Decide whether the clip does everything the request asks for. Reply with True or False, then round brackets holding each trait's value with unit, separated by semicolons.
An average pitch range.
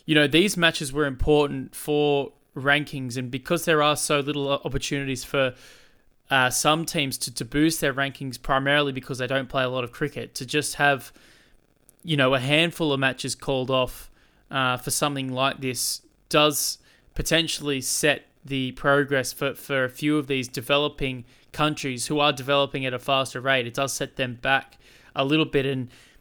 False (2.1 semitones)